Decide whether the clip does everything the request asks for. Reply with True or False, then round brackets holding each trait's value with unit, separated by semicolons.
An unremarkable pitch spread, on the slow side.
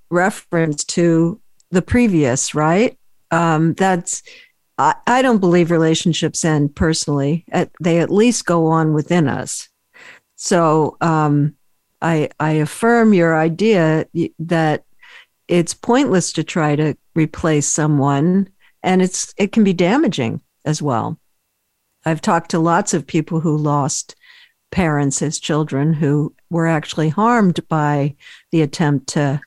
True (3.3 semitones; 130 wpm)